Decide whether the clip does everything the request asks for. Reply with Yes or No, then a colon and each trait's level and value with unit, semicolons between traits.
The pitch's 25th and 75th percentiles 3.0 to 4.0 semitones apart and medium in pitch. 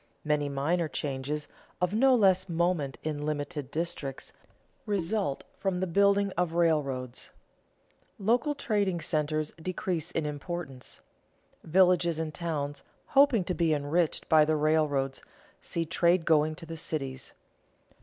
Yes: average, 3.4 semitones; medium, 160 Hz